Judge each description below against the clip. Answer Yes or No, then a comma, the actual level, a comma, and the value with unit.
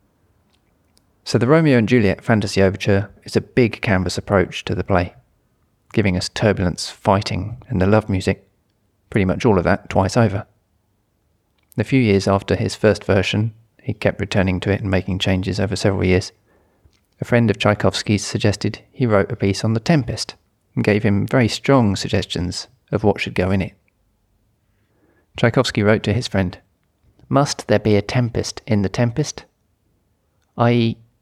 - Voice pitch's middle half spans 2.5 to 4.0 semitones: Yes, average, 2.8 semitones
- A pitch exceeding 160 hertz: No, low, 105 Hz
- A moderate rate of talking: Yes, average, 165 wpm